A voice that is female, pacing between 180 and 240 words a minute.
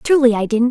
No: female; fast, 255 wpm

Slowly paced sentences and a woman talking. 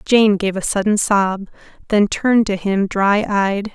No: average, 175 wpm; female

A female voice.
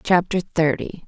Yes: female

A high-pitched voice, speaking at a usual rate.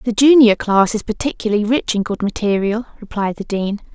Yes: high, 215 Hz; average, 185 wpm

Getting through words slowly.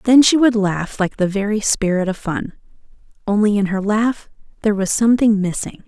No: average, 185 wpm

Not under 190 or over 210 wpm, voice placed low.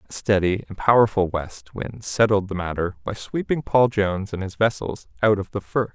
Yes: average, 200 wpm; low, 100 Hz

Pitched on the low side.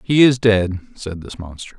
Yes: low, 105 Hz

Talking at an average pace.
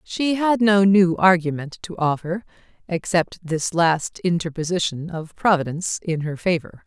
No: slow, 130 wpm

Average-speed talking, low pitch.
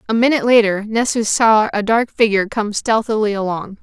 No: average, 175 wpm; high, 215 Hz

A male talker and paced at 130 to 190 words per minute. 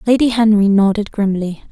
No: female; average, 140 wpm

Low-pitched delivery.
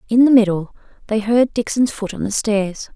No: high, 220 Hz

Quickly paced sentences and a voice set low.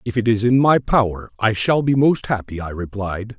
Yes: fast, 230 wpm; low, 110 Hz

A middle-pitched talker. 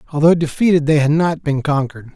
Yes: medium, 150 Hz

